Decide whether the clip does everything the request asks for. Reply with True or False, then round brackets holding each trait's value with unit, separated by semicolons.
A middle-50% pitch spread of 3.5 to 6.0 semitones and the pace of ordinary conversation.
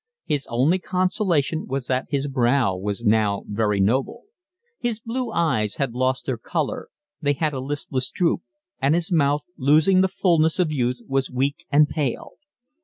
True (4.7 semitones; 165 wpm)